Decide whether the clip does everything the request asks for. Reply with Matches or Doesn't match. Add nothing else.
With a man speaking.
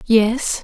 Doesn't match